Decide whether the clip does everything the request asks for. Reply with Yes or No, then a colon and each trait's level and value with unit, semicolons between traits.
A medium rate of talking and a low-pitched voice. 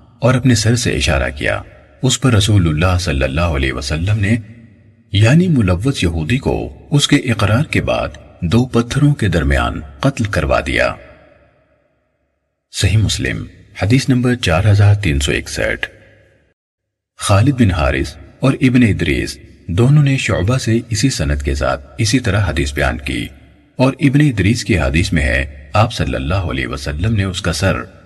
Yes: average, 160 wpm; low, 100 Hz